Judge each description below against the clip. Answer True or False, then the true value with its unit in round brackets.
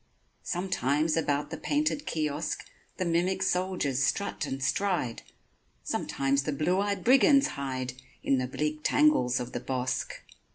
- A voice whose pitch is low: False (150 Hz)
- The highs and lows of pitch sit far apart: True (5.7 semitones)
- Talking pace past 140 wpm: False (135 wpm)